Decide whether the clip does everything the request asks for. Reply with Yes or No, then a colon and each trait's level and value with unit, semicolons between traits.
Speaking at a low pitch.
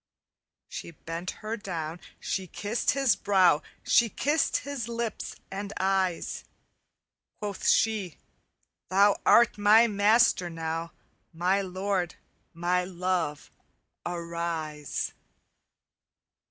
No: high, 190 Hz